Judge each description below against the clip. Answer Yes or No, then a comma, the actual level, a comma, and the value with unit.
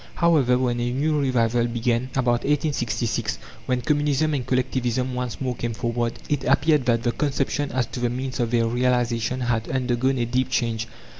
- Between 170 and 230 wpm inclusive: Yes, average, 175 wpm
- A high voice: No, low, 125 Hz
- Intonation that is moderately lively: No, narrow, 2.0 semitones